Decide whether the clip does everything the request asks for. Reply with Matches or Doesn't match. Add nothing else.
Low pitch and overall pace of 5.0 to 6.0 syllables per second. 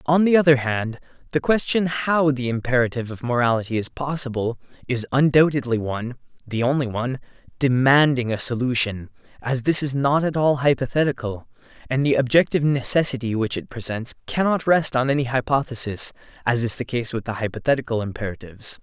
Matches